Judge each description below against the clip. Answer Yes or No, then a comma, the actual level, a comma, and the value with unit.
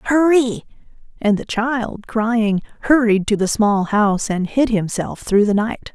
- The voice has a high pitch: Yes, high, 220 Hz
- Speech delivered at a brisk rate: No, average, 160 wpm